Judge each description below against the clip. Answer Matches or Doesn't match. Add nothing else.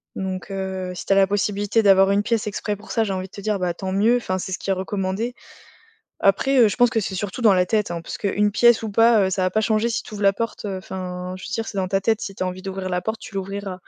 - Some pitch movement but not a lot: Doesn't match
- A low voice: Doesn't match